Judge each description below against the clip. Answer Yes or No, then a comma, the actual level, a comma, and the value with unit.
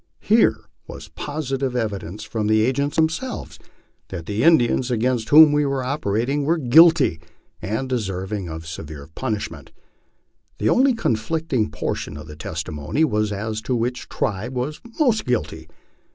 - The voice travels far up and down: Yes, wide, 6.0 semitones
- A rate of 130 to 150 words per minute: Yes, average, 145 wpm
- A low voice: Yes, low, 120 Hz